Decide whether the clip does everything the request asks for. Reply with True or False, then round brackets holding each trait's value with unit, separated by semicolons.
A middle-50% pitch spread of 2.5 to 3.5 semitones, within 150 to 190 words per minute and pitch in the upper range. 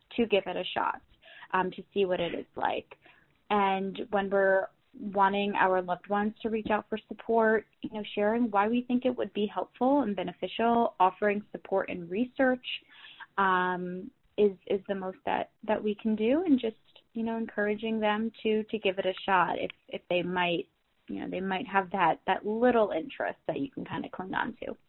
False (2.9 semitones; 200 wpm; 210 Hz)